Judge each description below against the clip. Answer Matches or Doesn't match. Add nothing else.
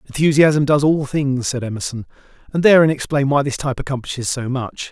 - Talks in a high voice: Doesn't match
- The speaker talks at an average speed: Matches